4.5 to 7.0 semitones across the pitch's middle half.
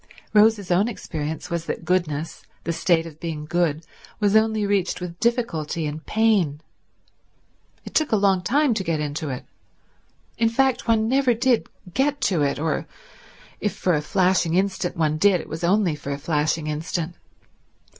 Yes: wide, 5.6 semitones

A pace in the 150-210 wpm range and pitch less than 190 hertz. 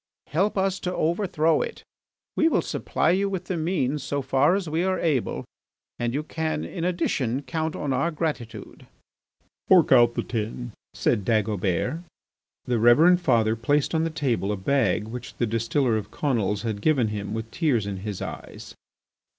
Yes: average, 170 wpm; low, 135 Hz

